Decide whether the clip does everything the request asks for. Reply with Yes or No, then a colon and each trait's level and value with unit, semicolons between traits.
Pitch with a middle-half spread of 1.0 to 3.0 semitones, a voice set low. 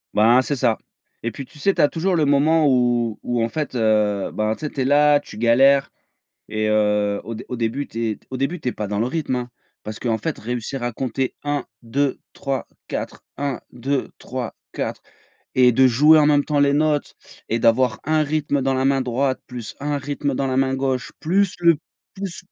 No: average, 3.7 semitones; low, 130 Hz